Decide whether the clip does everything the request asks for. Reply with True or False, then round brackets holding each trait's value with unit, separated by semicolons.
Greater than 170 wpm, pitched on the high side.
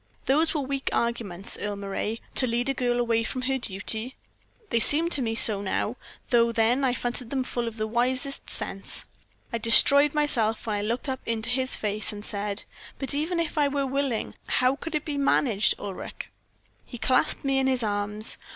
True (190 wpm; 240 Hz)